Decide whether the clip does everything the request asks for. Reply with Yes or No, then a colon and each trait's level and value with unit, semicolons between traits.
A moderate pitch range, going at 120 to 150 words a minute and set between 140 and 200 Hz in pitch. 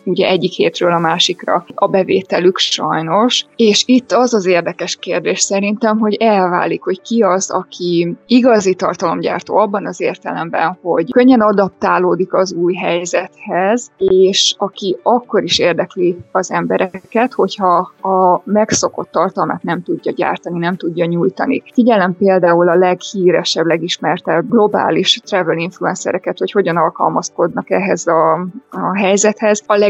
Yes: average, 3.3 semitones; average, 130 wpm; high, 190 Hz